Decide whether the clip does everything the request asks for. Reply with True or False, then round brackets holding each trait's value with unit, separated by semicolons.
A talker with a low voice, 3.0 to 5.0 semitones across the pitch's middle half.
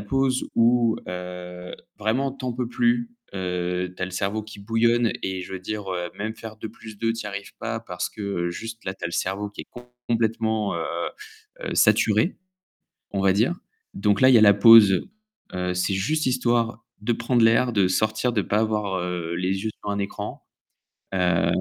True (105 Hz; 3.6 semitones)